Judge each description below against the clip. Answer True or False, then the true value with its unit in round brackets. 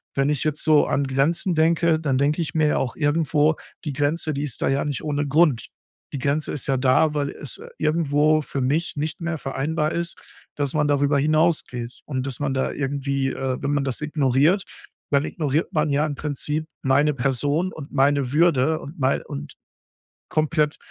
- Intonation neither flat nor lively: False (2.2 semitones)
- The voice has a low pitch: False (145 Hz)